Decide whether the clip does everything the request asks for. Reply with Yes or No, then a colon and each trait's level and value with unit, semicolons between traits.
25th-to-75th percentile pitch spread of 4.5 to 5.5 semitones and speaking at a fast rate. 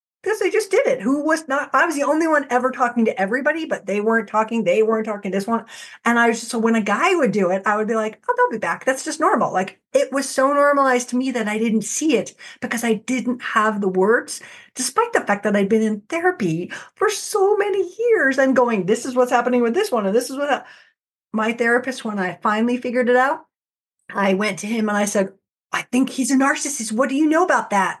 Yes: average, 5.2 semitones; fast, 255 wpm